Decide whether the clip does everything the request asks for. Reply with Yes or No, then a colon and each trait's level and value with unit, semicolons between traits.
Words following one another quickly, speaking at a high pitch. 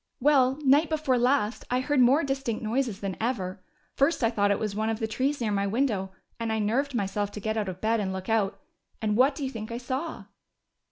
Yes: fast, 230 wpm; high, 230 Hz